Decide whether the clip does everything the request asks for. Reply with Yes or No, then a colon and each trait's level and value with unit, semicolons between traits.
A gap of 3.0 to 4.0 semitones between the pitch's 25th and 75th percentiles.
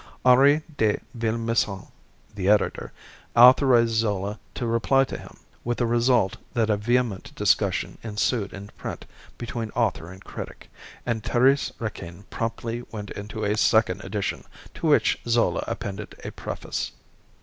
No: narrow, 2.6 semitones